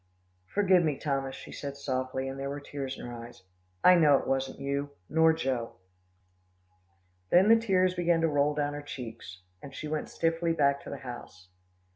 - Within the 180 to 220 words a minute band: Yes, average, 185 wpm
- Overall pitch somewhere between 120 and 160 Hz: Yes, medium, 140 Hz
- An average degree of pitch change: Yes, average, 3.5 semitones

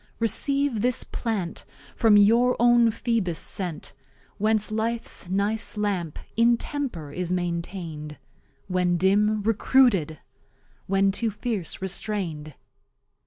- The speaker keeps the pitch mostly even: No, average, 4.3 semitones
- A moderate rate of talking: No, slow, 105 wpm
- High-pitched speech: Yes, high, 205 Hz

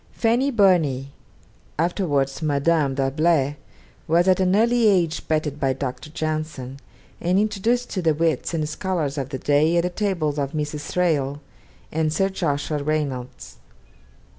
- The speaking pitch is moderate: Yes, medium, 155 Hz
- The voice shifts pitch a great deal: No, average, 4.1 semitones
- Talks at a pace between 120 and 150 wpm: Yes, average, 140 wpm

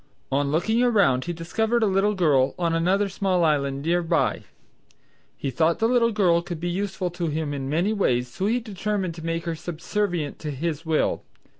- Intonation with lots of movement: No, average, 4.3 semitones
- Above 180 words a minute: Yes, average, 190 wpm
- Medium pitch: Yes, medium, 170 Hz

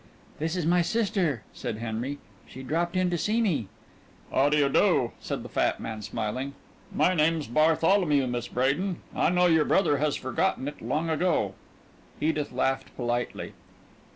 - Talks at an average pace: Yes, average, 160 wpm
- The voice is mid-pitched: Yes, medium, 150 Hz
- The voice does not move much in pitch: No, average, 5.0 semitones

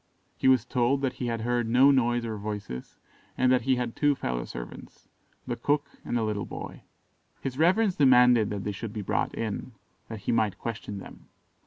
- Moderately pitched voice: No, low, 120 Hz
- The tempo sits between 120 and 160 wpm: No, average, 195 wpm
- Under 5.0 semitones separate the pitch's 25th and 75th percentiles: Yes, average, 3.5 semitones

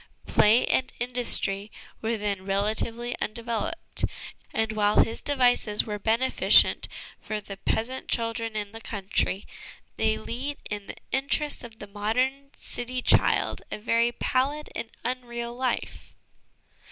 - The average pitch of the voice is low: No, high, 230 Hz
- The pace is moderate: No, slow, 130 wpm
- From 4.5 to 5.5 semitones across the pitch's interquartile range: No, average, 2.9 semitones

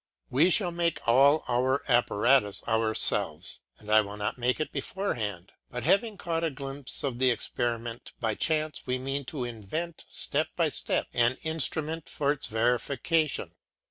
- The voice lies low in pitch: Yes, low, 130 Hz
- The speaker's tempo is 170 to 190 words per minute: No, average, 155 wpm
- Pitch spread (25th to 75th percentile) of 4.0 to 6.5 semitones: Yes, average, 4.9 semitones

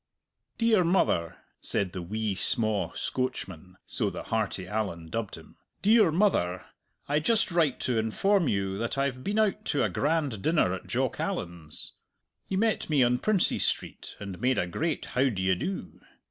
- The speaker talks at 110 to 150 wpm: No, average, 165 wpm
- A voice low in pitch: Yes, low, 125 Hz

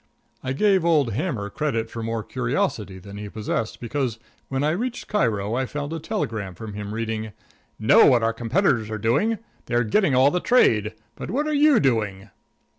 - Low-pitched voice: Yes, low, 115 Hz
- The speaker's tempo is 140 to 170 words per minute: No, average, 190 wpm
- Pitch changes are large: Yes, wide, 6.4 semitones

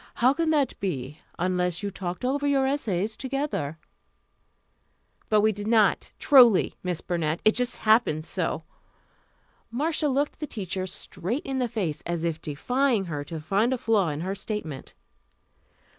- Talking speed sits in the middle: Yes, average, 155 wpm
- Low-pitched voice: No, high, 210 Hz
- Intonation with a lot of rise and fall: Yes, wide, 6.9 semitones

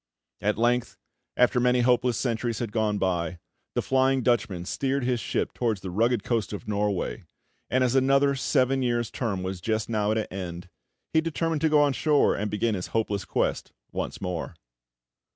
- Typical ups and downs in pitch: Yes, average, 4.0 semitones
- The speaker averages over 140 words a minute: Yes, average, 180 wpm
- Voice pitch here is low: Yes, low, 115 Hz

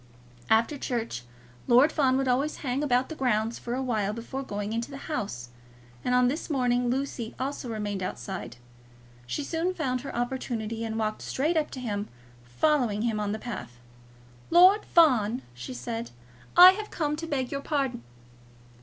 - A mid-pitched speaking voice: No, high, 245 Hz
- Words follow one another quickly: No, average, 165 wpm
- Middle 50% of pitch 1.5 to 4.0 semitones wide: No, average, 4.6 semitones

